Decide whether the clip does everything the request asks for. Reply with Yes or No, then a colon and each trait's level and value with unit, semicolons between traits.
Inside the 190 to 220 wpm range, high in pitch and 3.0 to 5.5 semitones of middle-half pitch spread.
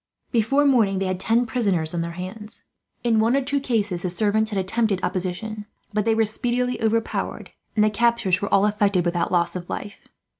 Yes: average, 195 wpm; high, 210 Hz; average, 3.6 semitones